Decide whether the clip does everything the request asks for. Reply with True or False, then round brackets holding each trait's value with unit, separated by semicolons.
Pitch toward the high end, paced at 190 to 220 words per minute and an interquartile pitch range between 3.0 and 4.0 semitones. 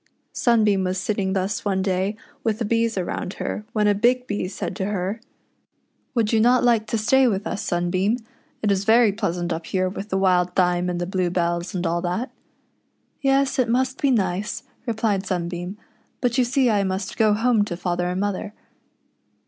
True (200 Hz; 195 wpm; 3.7 semitones)